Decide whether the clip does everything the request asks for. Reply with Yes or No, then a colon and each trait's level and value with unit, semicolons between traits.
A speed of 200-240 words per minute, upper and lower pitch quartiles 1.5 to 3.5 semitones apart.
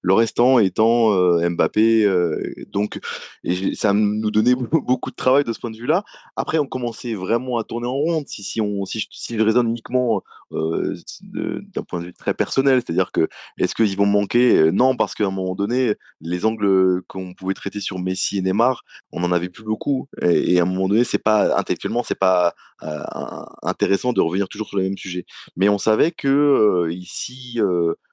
No: average, 205 wpm; average, 4.2 semitones